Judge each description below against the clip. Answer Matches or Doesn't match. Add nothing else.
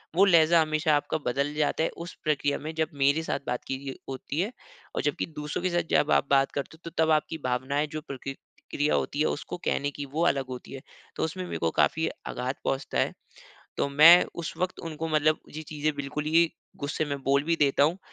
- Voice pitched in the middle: Matches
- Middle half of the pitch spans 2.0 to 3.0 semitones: Matches